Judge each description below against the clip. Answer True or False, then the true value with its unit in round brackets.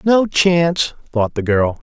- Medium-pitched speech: True (150 Hz)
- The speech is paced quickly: False (160 wpm)